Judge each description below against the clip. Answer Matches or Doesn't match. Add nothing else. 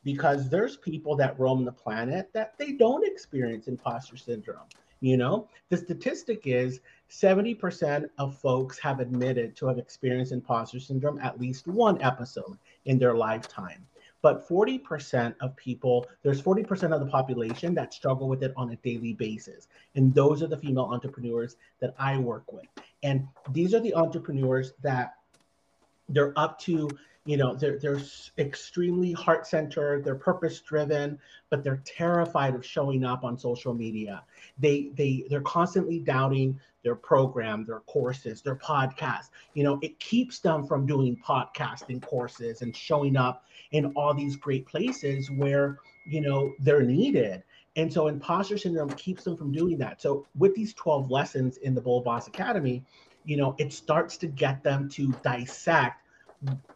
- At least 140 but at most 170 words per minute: Matches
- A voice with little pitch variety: Doesn't match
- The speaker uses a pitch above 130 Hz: Matches